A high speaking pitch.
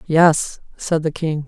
No: medium, 155 Hz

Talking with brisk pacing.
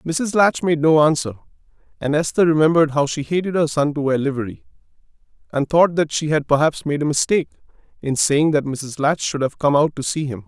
Yes: fast, 210 wpm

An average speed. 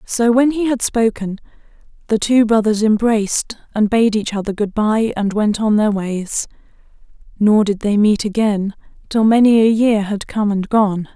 Yes: average, 175 wpm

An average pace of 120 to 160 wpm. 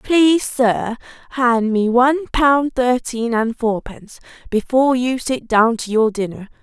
Yes: average, 155 wpm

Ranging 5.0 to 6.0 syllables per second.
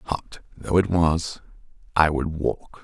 No: 3.2 syllables/s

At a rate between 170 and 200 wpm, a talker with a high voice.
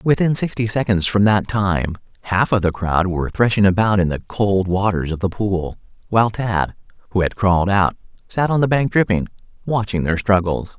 No: average, 190 wpm; low, 100 Hz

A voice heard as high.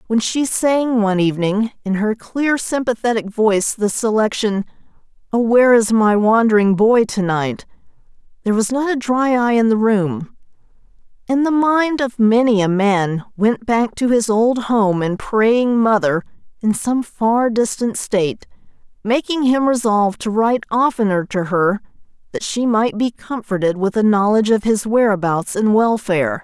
Yes: high, 220 Hz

